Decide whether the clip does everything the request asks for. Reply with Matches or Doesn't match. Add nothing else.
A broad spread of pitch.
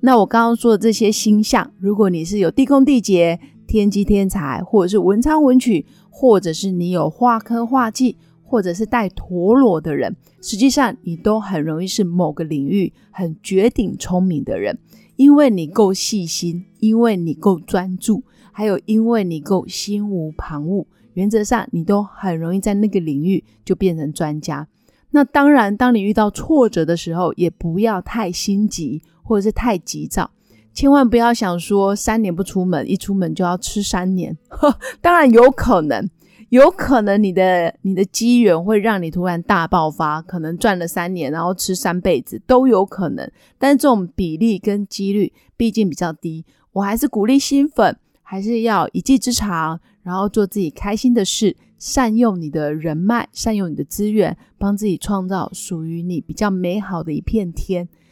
Doesn't match